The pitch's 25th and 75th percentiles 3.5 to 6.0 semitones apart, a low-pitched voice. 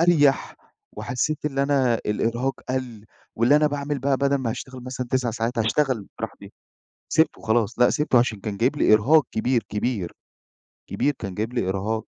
Yes: average, 3.8 semitones; low, 125 Hz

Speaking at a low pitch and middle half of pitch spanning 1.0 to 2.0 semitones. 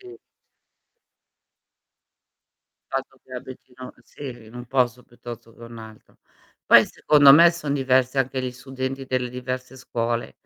Yes: low, 130 Hz; narrow, 1.7 semitones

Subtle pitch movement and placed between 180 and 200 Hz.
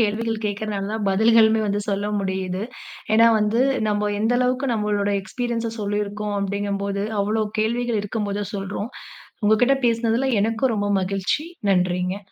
No: narrow, 2.0 semitones; high, 210 Hz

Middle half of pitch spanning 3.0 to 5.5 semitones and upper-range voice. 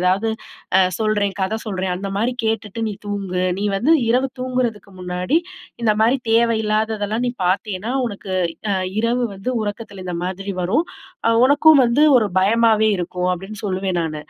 Yes: average, 3.4 semitones; high, 210 Hz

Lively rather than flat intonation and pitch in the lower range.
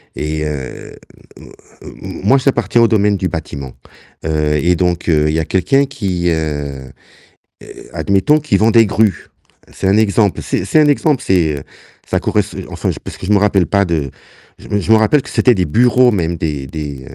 Yes: wide, 6.2 semitones; very low, 95 Hz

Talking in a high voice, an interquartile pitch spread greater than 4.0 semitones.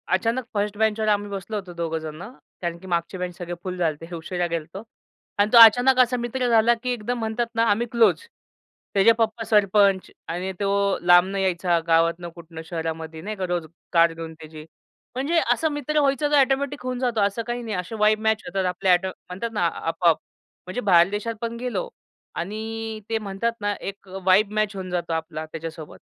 Yes: high, 195 Hz; average, 4.8 semitones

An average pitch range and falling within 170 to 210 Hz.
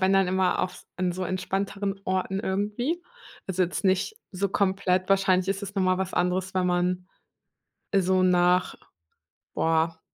No: narrow, 1.3 semitones; medium, 185 Hz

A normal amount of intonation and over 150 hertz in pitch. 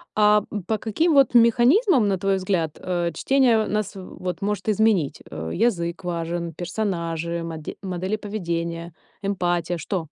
Yes: average, 4.1 semitones; medium, 185 Hz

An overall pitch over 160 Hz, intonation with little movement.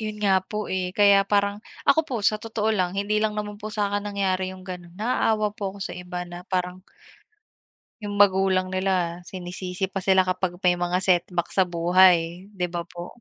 Yes: high, 190 Hz; narrow, 2.3 semitones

